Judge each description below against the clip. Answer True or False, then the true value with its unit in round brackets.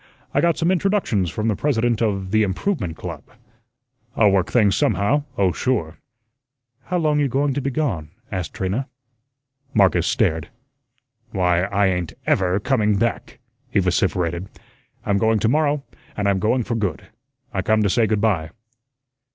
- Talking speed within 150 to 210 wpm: True (160 wpm)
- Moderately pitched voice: False (105 Hz)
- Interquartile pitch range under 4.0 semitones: False (5.3 semitones)